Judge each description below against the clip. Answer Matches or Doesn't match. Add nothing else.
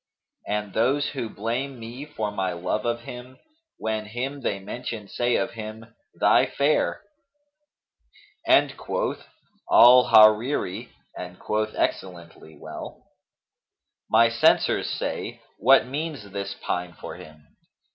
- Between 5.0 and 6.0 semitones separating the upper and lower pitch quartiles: Doesn't match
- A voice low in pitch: Matches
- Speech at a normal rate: Doesn't match